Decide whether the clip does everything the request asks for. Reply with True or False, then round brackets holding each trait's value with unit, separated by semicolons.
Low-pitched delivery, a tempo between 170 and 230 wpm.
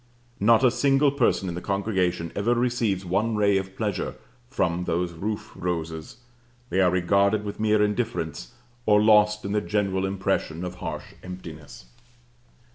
False (100 Hz; 150 wpm)